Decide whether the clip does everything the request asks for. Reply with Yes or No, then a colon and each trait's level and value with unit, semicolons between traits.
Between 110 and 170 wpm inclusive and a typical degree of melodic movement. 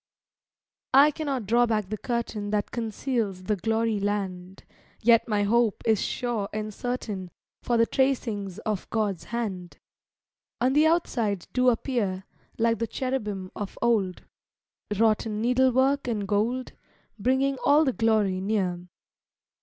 Yes: average, 140 wpm; average, 3.4 semitones